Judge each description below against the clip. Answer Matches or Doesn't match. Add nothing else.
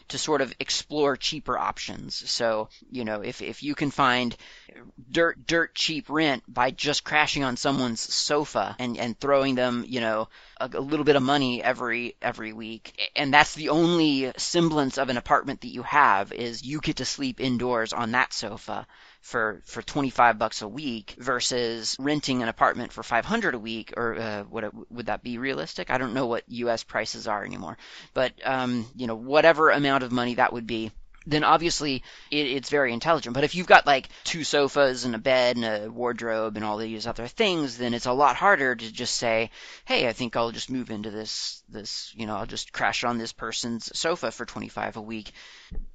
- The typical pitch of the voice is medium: Doesn't match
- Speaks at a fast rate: Matches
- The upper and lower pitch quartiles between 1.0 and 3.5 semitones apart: Doesn't match